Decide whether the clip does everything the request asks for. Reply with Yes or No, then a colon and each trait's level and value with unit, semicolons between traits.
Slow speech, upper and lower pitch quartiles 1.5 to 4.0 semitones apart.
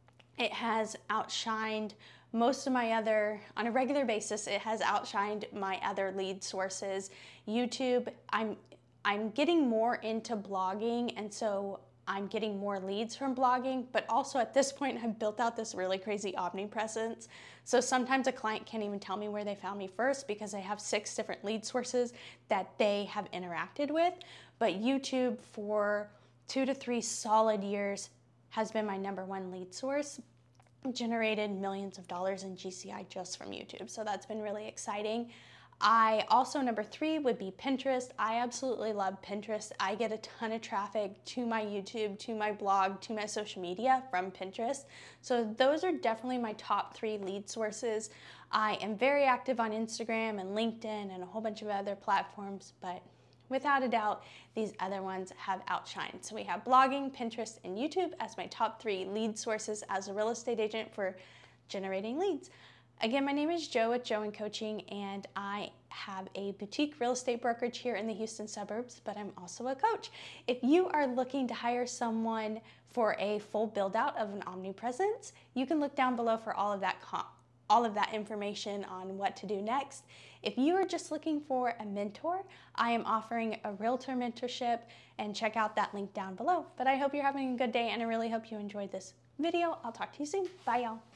No: average, 190 wpm; average, 3.5 semitones